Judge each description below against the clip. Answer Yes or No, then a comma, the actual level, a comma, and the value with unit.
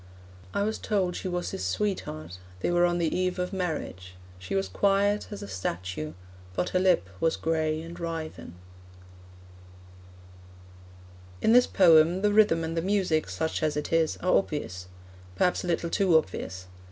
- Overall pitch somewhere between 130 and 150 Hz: No, medium, 165 Hz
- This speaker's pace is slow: No, average, 165 wpm